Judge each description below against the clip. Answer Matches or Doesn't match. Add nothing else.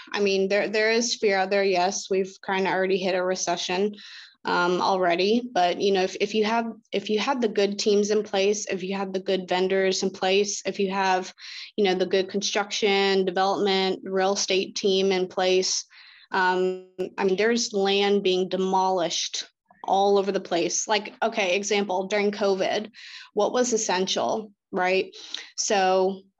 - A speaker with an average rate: Matches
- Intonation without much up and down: Matches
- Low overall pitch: Doesn't match